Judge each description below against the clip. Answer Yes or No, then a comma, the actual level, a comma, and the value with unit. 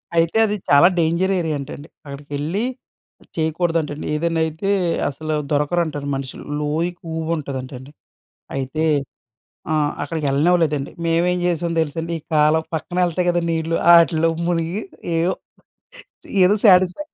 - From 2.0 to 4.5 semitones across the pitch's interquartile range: Yes, average, 2.8 semitones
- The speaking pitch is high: No, medium, 160 Hz